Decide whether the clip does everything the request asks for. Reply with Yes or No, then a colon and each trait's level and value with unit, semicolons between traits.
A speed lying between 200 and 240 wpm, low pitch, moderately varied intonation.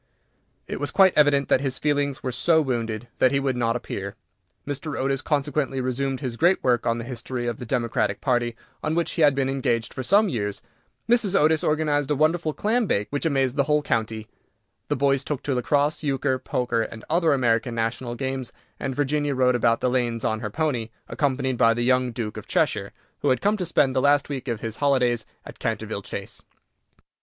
Yes: fast, 205 wpm; low, 130 Hz; average, 3.4 semitones